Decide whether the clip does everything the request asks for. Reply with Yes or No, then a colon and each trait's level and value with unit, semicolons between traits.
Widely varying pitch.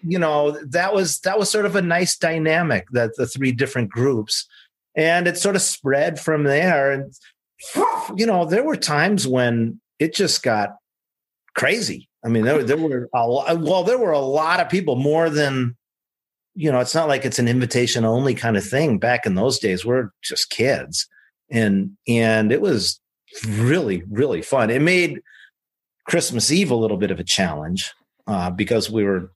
Yes: wide, 6.8 semitones